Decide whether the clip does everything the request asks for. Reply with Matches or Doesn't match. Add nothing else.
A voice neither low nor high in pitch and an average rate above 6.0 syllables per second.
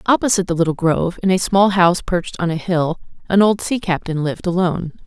Matches